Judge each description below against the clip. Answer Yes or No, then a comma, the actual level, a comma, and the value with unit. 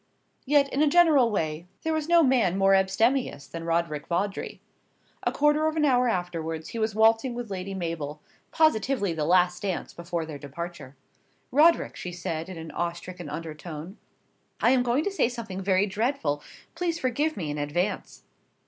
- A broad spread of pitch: Yes, wide, 7.4 semitones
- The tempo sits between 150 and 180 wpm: Yes, average, 175 wpm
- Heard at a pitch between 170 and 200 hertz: Yes, high, 190 Hz